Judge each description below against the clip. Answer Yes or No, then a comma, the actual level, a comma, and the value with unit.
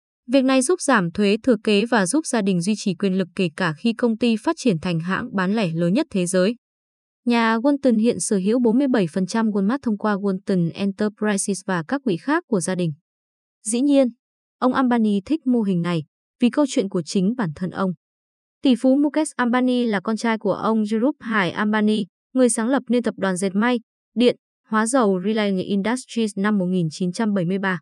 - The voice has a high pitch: Yes, high, 215 Hz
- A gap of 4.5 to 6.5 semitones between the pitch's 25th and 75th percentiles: No, average, 4.1 semitones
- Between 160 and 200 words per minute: Yes, average, 195 wpm